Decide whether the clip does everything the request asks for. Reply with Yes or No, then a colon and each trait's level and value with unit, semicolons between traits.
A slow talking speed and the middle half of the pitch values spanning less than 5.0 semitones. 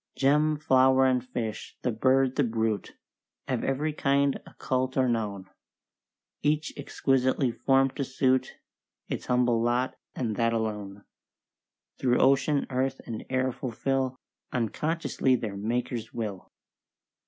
Yes: slow, 120 wpm; narrow, 2.6 semitones